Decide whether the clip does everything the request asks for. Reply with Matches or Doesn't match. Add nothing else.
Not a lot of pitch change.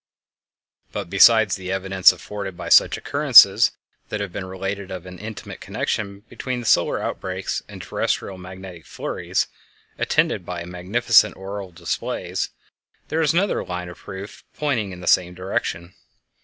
Matches